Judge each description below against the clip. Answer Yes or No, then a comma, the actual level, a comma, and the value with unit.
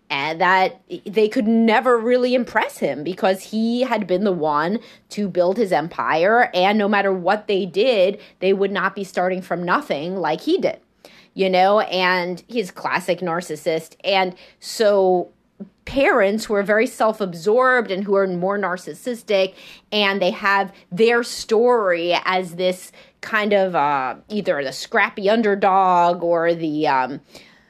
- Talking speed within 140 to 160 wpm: Yes, average, 150 wpm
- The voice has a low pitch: No, high, 195 Hz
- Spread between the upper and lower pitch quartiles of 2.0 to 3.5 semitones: Yes, average, 3.2 semitones